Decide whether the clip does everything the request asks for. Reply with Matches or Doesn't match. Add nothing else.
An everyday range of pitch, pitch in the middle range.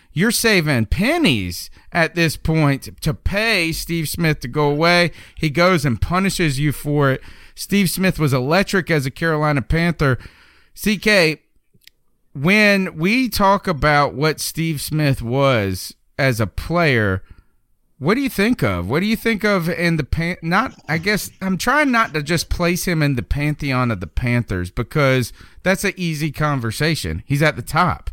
Doesn't match